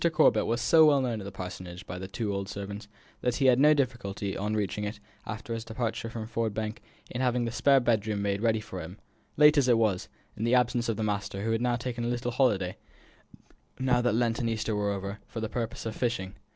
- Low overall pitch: Yes, low, 115 Hz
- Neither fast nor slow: No, fast, 240 wpm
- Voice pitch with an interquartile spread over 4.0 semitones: No, average, 3.2 semitones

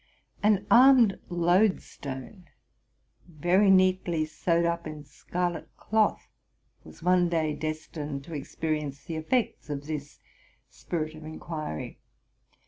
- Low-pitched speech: No, medium, 165 Hz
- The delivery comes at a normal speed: No, slow, 110 wpm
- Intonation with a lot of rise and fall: No, average, 3.1 semitones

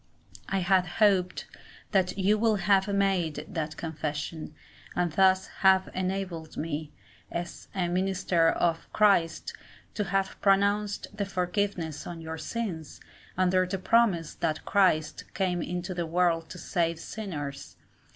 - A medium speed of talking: No, slow, 130 wpm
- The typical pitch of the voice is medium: Yes, medium, 180 Hz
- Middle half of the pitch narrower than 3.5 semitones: Yes, average, 2.9 semitones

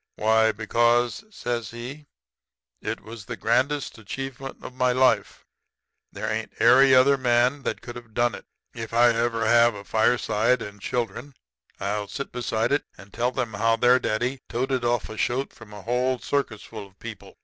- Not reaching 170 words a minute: No, average, 175 wpm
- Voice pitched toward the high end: No, low, 120 Hz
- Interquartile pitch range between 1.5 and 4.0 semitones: Yes, narrow, 2.4 semitones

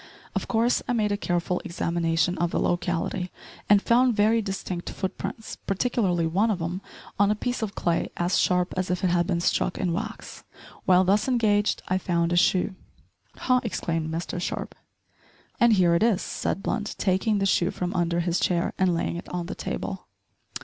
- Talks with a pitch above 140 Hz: Yes, medium, 185 Hz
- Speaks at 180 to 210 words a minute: Yes, average, 190 wpm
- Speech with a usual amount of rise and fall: Yes, average, 3.2 semitones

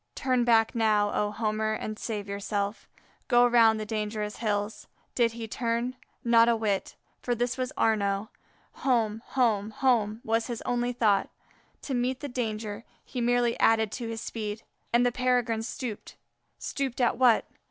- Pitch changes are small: Yes, narrow, 2.2 semitones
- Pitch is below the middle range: No, high, 225 Hz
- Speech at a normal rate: Yes, average, 160 wpm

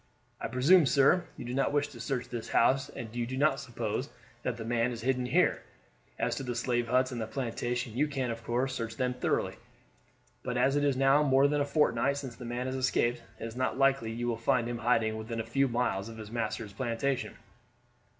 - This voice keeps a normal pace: No, fast, 220 wpm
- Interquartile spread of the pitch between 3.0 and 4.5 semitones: No, narrow, 2.5 semitones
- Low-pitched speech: Yes, low, 125 Hz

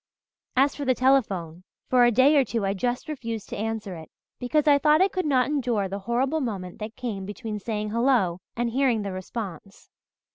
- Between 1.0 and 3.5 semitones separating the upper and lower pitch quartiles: No, average, 4.9 semitones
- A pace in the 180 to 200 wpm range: Yes, average, 195 wpm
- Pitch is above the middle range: Yes, high, 235 Hz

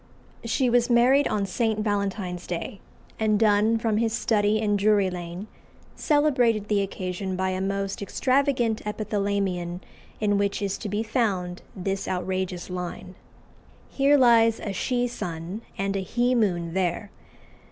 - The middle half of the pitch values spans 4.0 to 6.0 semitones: No, average, 3.3 semitones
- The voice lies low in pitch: No, high, 205 Hz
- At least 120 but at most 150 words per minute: Yes, average, 140 wpm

